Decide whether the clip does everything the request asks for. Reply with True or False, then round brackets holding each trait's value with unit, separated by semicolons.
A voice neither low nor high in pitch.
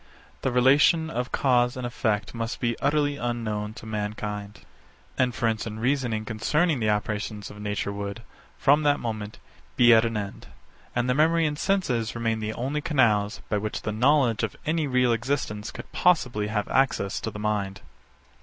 False (115 Hz)